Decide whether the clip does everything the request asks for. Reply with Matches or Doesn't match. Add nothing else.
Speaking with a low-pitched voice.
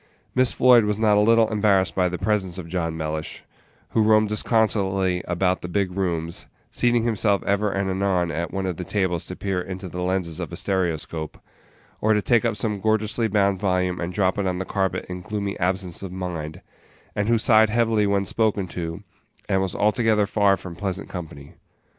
Matches